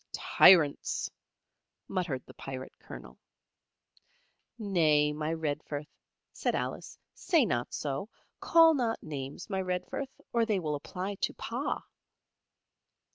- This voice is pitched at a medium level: Yes, medium, 165 Hz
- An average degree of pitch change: No, wide, 5.9 semitones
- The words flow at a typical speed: No, slow, 110 wpm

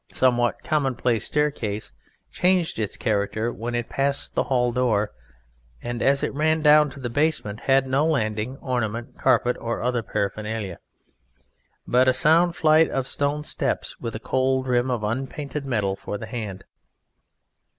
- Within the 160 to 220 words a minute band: No, average, 150 wpm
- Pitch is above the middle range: No, low, 125 Hz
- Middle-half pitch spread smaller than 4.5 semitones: Yes, average, 3.9 semitones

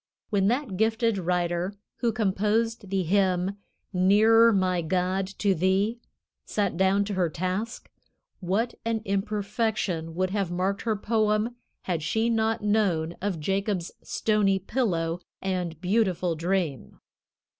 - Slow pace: Yes, slow, 125 wpm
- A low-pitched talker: No, high, 195 Hz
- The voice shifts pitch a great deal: No, average, 3.2 semitones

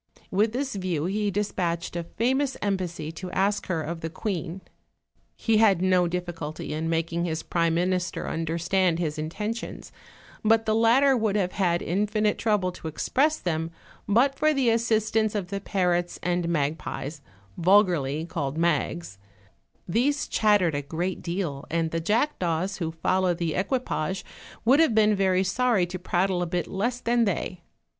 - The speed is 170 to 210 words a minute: No, average, 160 wpm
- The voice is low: No, medium, 185 Hz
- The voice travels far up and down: No, average, 4.2 semitones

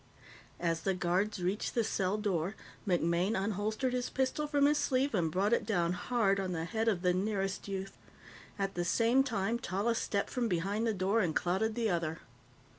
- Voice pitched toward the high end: Yes, high, 200 Hz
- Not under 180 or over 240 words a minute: Yes, average, 190 wpm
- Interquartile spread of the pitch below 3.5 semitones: No, average, 4.0 semitones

